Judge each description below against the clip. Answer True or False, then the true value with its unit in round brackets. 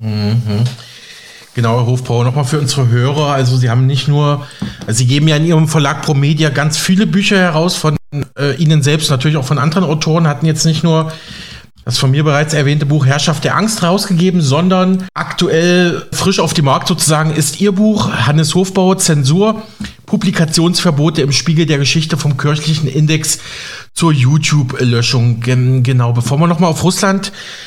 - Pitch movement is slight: False (3.6 semitones)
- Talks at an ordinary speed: True (170 wpm)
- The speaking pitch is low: False (155 Hz)